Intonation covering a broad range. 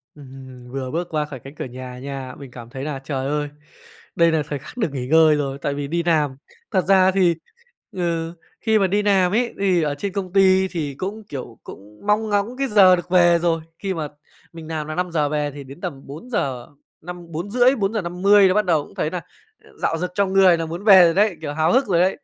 No: average, 4.8 semitones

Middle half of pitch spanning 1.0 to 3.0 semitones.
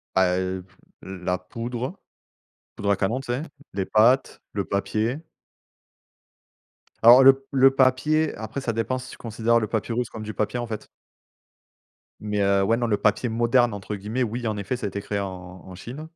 No: average, 3.8 semitones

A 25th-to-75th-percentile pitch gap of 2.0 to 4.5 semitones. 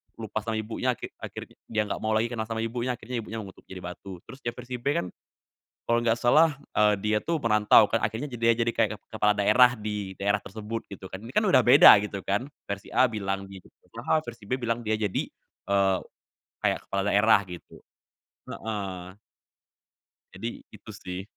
Yes: average, 2.8 semitones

